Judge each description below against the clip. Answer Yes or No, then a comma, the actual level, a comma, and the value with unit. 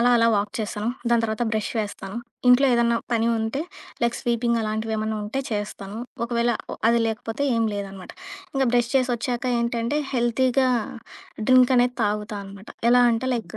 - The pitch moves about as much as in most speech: No, narrow, 2.1 semitones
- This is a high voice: Yes, high, 235 Hz